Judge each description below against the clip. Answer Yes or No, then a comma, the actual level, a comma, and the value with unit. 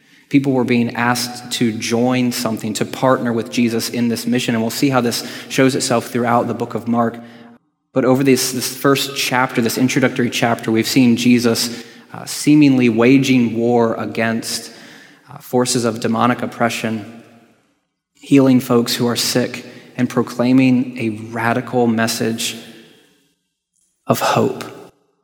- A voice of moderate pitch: No, low, 120 Hz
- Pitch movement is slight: Yes, narrow, 1.5 semitones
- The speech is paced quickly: No, average, 145 wpm